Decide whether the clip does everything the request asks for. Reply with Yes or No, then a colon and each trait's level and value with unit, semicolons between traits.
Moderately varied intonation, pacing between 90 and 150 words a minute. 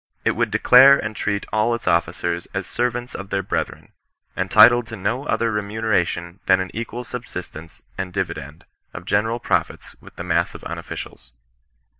No: average, 4.1 semitones; average, 165 wpm